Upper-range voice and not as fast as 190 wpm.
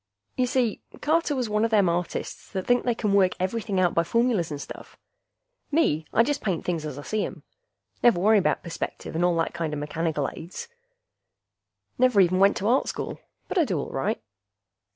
No: high, 195 Hz; average, 195 wpm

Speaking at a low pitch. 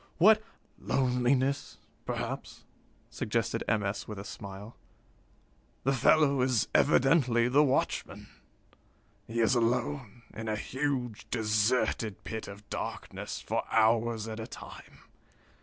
Yes: low, 115 Hz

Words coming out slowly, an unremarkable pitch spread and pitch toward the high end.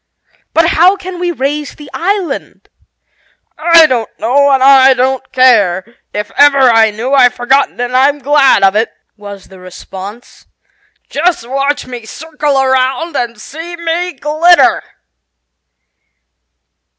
Yes: slow, 130 wpm; average, 4.7 semitones; very high, 270 Hz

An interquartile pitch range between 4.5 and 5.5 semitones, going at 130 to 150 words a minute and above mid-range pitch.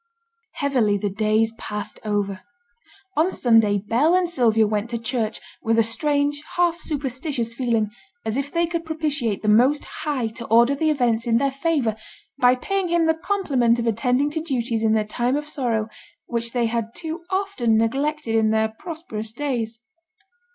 No: average, 5.0 semitones; average, 170 wpm; high, 240 Hz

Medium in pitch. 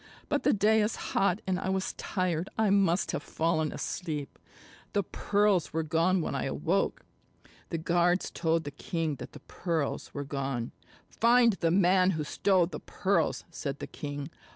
Yes: medium, 175 Hz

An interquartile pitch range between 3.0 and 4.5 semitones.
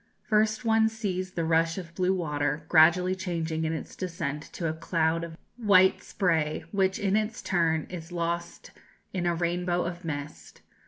No: narrow, 2.6 semitones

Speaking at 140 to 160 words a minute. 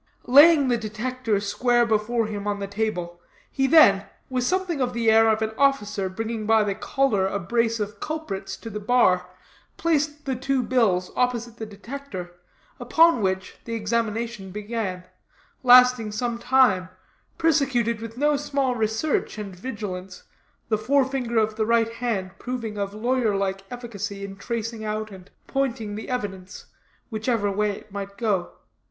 Yes: average, 155 wpm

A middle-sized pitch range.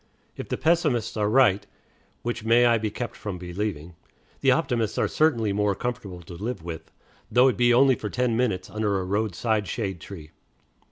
Yes: average, 3.9 semitones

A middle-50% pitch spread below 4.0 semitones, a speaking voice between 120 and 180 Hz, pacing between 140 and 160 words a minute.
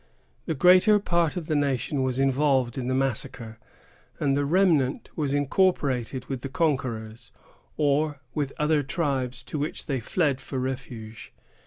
Yes: average, 2.9 semitones; medium, 140 Hz; average, 150 wpm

